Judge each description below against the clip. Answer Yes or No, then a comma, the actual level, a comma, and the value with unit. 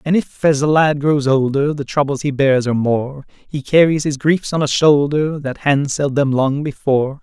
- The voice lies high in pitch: No, medium, 145 Hz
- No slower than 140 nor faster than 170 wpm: No, fast, 205 wpm